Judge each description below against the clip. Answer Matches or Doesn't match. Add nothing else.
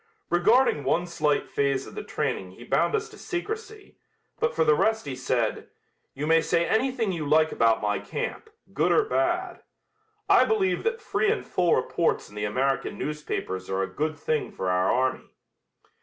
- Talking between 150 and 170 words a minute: Doesn't match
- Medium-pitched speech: Matches